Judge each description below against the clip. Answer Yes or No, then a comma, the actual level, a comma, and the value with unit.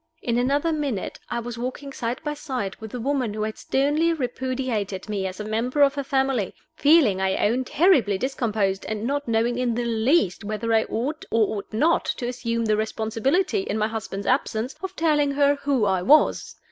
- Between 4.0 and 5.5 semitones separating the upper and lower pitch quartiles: Yes, average, 4.5 semitones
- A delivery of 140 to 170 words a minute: No, average, 195 wpm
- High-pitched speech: Yes, high, 245 Hz